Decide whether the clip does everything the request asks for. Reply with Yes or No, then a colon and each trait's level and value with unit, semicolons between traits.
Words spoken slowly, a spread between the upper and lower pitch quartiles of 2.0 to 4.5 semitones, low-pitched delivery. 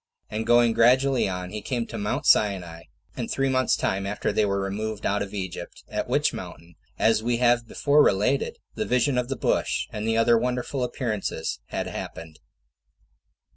No: average, 175 wpm; average, 3.9 semitones; low, 110 Hz